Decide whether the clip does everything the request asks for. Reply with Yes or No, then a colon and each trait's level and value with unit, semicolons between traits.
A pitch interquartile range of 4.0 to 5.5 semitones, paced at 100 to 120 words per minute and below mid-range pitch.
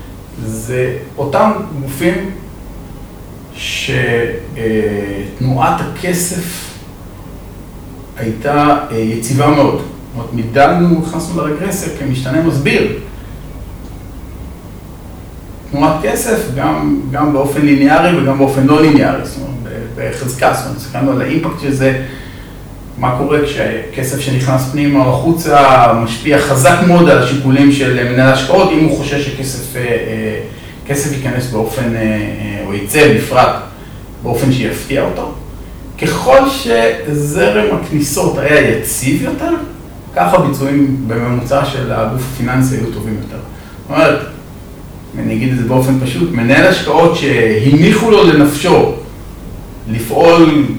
Yes: average, 4.6 semitones; average, 110 wpm; low, 130 Hz